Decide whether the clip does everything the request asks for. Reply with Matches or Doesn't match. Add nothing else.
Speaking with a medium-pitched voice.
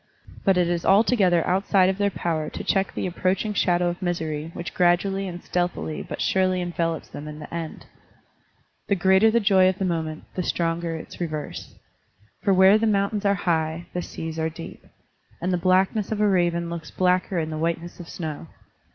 Matches